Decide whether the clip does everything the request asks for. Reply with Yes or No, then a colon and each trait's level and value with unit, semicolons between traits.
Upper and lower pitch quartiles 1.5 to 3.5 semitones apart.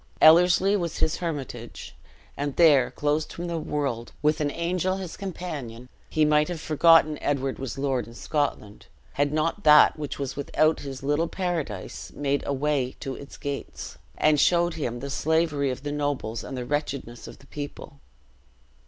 Yes: average, 2.9 semitones